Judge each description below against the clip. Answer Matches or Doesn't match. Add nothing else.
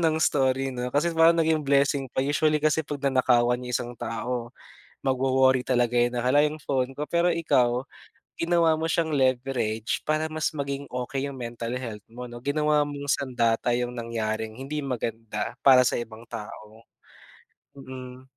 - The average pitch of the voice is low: Matches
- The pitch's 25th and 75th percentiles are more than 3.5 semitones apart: Doesn't match